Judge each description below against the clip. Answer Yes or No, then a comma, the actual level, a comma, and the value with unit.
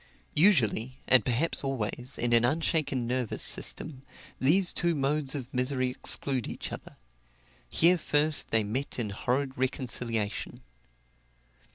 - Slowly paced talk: Yes, slow, 125 wpm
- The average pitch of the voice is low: Yes, low, 130 Hz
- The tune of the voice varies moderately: Yes, average, 3.3 semitones